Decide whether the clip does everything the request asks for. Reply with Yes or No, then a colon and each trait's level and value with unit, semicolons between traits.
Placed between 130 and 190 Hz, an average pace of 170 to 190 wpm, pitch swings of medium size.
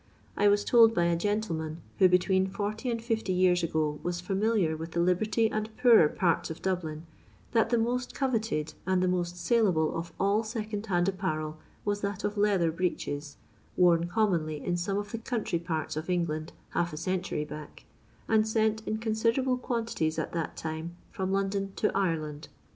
Yes: medium, 185 Hz; average, 175 wpm; average, 4.5 semitones